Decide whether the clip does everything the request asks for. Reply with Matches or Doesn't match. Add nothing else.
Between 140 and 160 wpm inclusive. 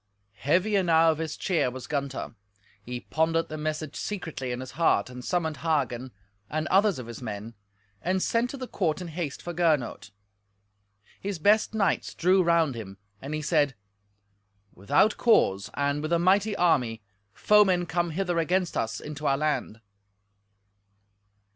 Matches